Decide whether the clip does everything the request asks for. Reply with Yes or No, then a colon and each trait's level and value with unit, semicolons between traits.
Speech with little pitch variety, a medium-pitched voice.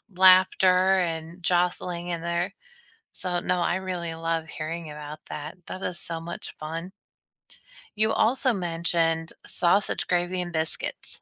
Yes: narrow, 2.0 semitones; medium, 175 Hz